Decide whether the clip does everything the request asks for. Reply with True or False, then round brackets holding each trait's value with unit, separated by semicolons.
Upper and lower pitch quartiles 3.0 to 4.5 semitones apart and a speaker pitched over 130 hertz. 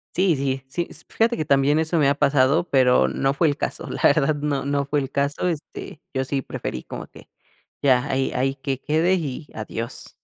False (2.6 semitones; 140 Hz)